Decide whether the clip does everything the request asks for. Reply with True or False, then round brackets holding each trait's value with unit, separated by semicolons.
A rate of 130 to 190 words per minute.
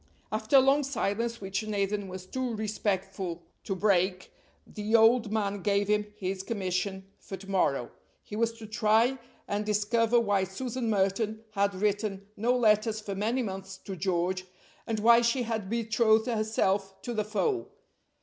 True (160 wpm)